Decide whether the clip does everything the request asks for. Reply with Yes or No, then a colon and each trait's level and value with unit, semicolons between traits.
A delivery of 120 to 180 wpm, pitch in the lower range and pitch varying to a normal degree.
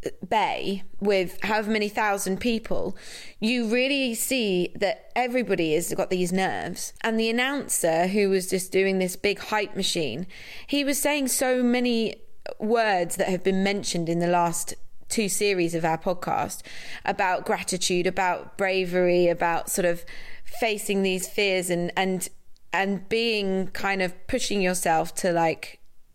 No: average, 145 wpm; high, 195 Hz; average, 3.6 semitones